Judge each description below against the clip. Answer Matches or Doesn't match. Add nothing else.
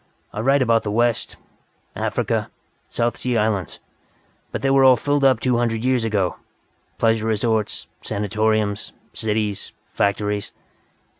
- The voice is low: Matches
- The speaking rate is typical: Doesn't match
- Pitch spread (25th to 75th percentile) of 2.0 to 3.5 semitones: Matches